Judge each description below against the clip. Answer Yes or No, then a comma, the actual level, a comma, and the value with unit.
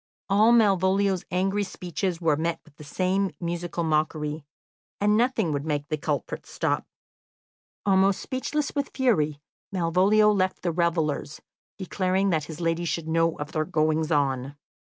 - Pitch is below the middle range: No, medium, 170 Hz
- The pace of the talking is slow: No, average, 145 wpm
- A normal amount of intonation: Yes, average, 3.9 semitones